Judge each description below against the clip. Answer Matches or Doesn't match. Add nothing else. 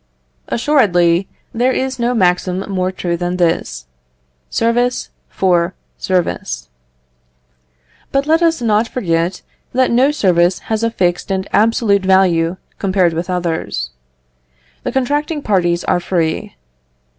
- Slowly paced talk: Matches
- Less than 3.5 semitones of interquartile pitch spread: Doesn't match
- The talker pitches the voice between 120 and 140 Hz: Doesn't match